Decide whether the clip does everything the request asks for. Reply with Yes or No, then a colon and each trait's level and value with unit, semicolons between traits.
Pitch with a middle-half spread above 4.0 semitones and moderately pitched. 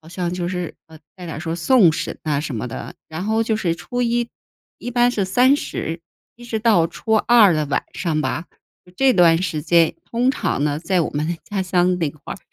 Yes: wide, 5.6 semitones; medium, 175 Hz